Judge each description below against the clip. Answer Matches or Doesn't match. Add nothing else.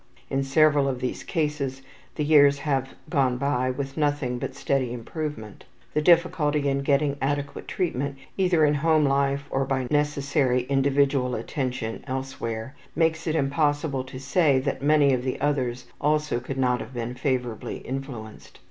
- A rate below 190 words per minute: Matches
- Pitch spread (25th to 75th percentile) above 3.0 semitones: Doesn't match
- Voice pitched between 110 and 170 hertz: Matches